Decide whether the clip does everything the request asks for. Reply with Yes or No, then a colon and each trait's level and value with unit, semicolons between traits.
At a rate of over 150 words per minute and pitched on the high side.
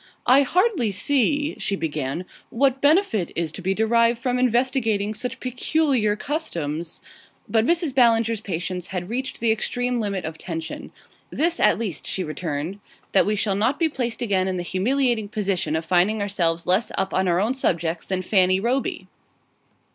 Yes: average, 170 wpm; high, 215 Hz